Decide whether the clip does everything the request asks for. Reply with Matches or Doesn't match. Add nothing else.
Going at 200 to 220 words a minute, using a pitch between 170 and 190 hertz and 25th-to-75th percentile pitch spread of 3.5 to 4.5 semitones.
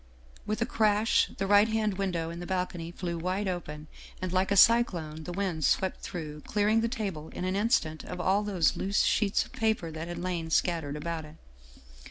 Matches